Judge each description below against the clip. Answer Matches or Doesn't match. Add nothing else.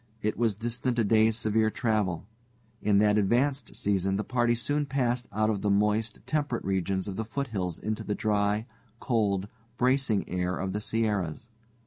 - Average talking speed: Matches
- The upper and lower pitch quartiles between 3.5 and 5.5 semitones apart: Doesn't match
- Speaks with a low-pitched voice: Matches